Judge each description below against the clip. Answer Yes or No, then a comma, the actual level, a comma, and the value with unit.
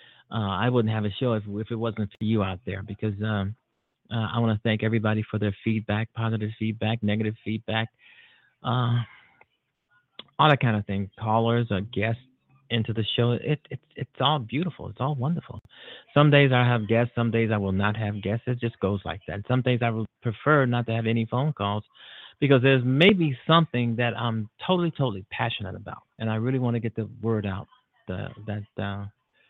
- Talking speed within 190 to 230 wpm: Yes, average, 200 wpm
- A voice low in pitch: Yes, low, 115 Hz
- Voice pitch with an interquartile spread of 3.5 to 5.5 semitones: No, average, 2.7 semitones